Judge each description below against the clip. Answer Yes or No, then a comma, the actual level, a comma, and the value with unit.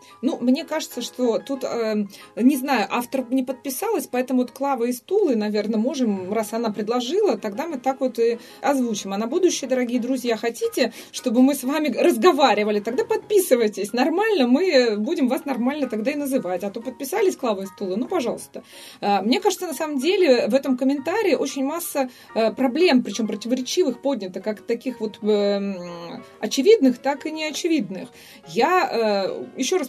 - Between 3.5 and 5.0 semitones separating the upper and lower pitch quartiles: Yes, average, 4.4 semitones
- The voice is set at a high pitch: Yes, very high, 260 Hz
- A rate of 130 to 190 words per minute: Yes, fast, 160 wpm